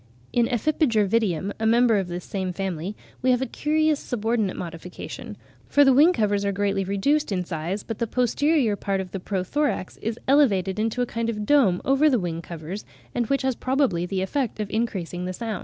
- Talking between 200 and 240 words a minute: Yes, fast, 205 wpm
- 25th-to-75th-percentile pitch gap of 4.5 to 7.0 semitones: Yes, average, 5.1 semitones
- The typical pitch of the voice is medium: No, high, 215 Hz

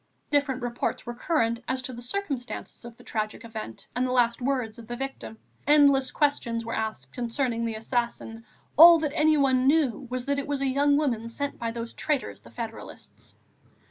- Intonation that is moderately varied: Yes, average, 3.5 semitones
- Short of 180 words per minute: No, average, 185 wpm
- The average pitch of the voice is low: No, very high, 250 Hz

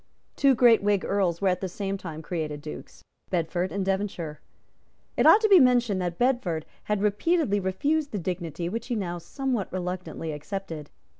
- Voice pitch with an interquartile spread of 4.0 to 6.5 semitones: Yes, average, 4.9 semitones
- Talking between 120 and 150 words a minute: No, average, 170 wpm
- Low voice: No, high, 190 Hz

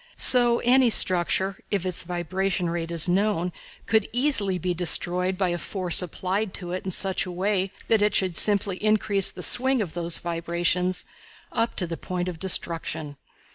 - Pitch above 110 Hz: Yes, medium, 185 Hz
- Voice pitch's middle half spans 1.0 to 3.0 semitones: Yes, average, 2.7 semitones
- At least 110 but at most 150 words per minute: No, average, 175 wpm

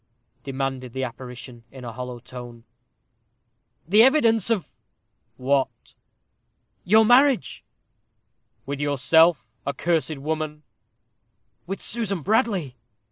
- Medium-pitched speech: Yes, medium, 145 Hz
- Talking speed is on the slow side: Yes, slow, 95 wpm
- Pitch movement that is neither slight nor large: No, wide, 7.5 semitones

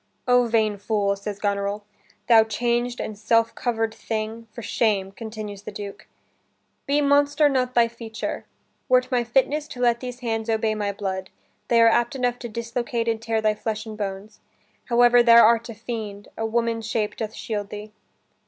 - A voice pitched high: Yes, high, 225 Hz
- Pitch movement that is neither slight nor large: No, narrow, 2.1 semitones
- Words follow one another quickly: No, average, 175 wpm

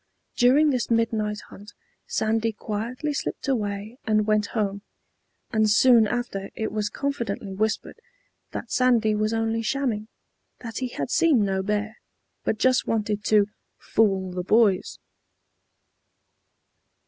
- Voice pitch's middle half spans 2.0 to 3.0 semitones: Yes, narrow, 2.4 semitones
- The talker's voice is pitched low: No, high, 220 Hz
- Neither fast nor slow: No, slow, 125 wpm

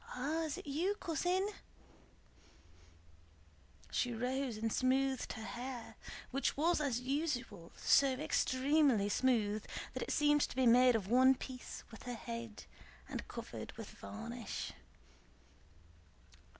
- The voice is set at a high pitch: Yes, very high, 255 Hz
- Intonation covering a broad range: No, average, 3.5 semitones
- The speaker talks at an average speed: No, slow, 125 wpm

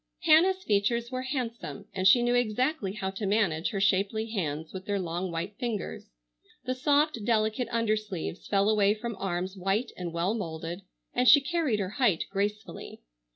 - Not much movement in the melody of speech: No, average, 4.0 semitones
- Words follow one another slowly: No, average, 165 wpm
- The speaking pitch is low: No, high, 210 Hz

